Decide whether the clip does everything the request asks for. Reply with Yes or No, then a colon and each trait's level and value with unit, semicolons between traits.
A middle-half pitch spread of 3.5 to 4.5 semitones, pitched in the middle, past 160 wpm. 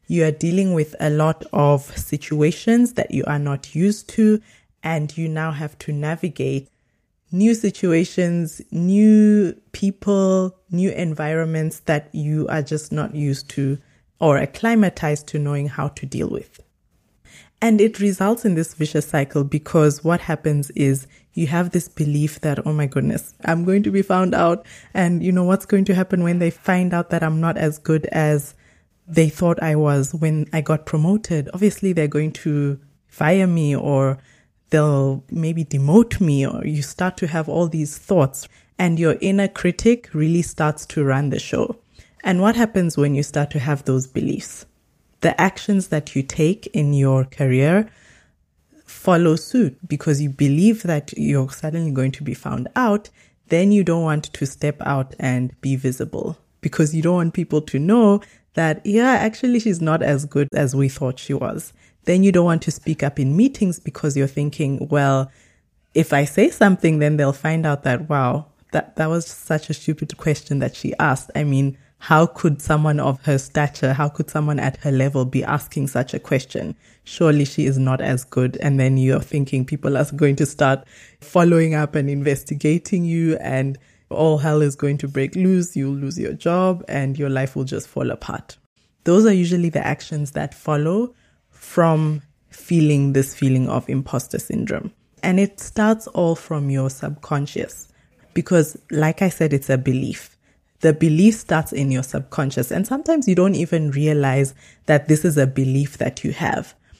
Yes: average, 3.8 semitones; medium, 155 Hz; average, 180 wpm